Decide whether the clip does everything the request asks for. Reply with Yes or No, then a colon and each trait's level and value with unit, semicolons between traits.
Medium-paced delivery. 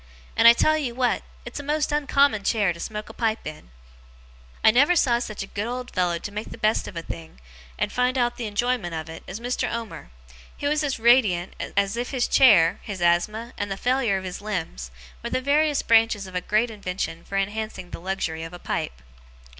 No: fast, 215 wpm